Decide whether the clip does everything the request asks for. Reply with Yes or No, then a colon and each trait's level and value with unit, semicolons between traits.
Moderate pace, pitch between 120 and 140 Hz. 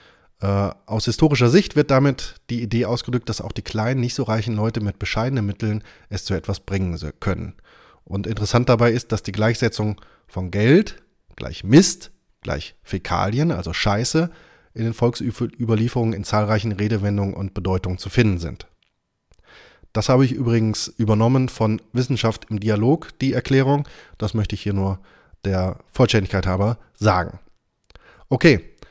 No: average, 150 wpm; low, 110 Hz